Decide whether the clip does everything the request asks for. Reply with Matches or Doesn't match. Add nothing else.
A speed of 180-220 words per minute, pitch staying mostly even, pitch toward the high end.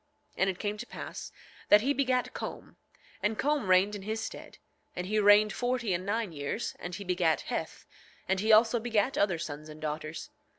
Doesn't match